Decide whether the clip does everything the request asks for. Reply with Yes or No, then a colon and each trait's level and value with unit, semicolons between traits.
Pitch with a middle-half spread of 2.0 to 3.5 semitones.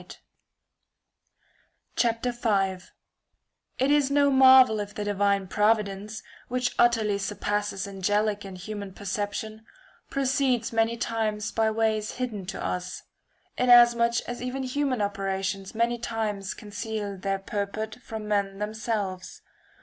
Yes: average, 2.9 semitones